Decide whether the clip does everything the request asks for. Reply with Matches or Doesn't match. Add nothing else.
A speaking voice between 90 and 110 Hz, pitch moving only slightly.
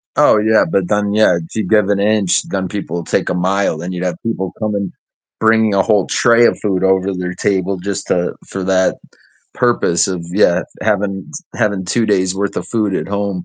Matches